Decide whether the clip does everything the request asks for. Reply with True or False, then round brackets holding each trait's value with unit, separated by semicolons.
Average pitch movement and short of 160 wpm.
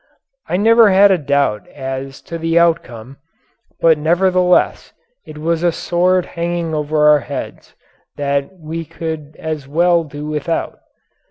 True (3.0 semitones; 140 wpm)